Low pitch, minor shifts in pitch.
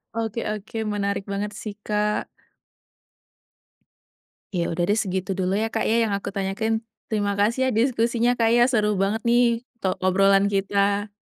No: high, 205 Hz; narrow, 2.1 semitones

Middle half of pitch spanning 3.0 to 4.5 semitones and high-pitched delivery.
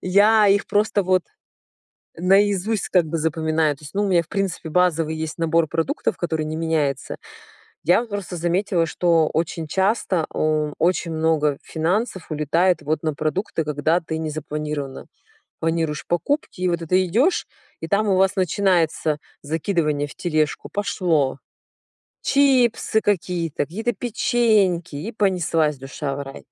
No: average, 3.7 semitones; medium, 170 Hz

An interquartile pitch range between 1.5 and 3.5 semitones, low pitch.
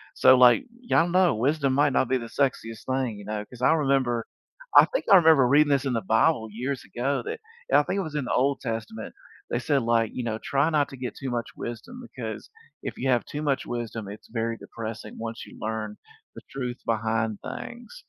No: average, 3.9 semitones; low, 125 Hz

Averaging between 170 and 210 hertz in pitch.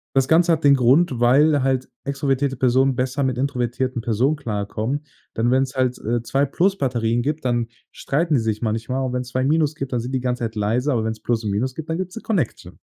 No: low, 130 Hz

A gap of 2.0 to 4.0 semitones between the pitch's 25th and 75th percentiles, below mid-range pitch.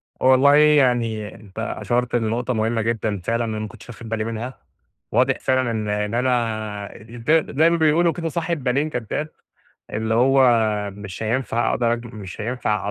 Yes: average, 3.2 semitones; low, 120 Hz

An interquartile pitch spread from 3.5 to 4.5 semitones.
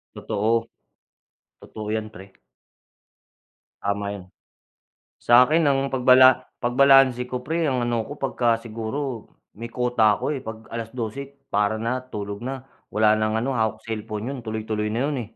No: average, 3.1 semitones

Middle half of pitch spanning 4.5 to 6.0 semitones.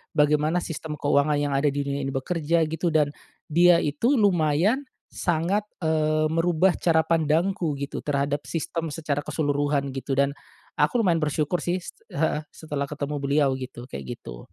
No: average, 2.7 semitones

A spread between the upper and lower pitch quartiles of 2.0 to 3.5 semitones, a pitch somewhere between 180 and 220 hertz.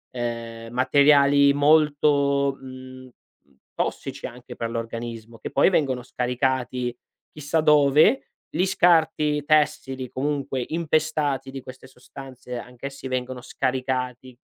No: narrow, 2.6 semitones; low, 135 Hz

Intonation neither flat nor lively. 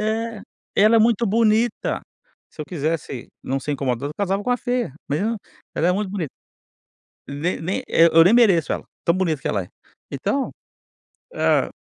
No: wide, 6.4 semitones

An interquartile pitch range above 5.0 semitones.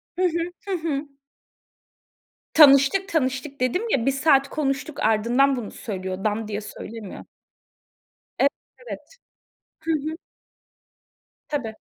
Yes: wide, 5.5 semitones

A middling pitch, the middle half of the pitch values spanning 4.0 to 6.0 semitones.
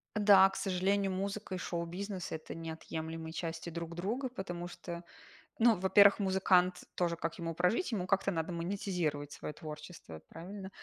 No: medium, 180 Hz; average, 2.9 semitones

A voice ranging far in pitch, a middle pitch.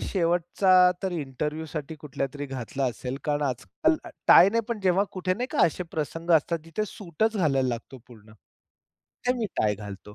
Yes: wide, 5.8 semitones; medium, 155 Hz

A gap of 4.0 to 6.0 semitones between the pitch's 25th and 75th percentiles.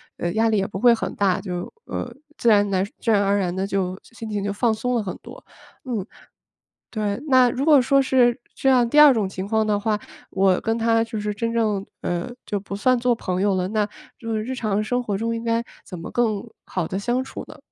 No: average, 3.2 semitones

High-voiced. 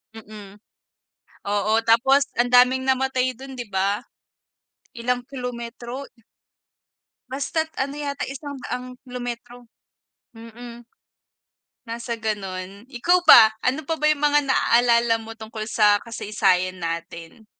Yes: high, 240 Hz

